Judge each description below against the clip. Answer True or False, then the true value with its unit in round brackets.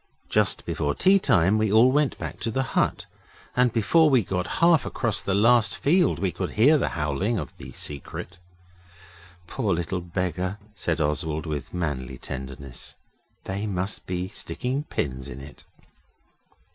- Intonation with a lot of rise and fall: True (7.1 semitones)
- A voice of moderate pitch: False (95 Hz)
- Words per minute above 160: False (155 wpm)